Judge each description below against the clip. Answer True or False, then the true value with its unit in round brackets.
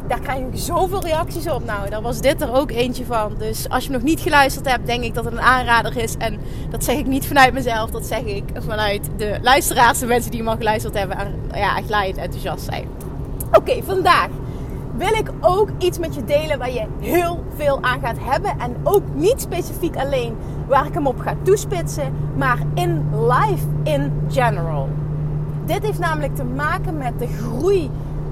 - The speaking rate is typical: False (205 wpm)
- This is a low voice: False (170 Hz)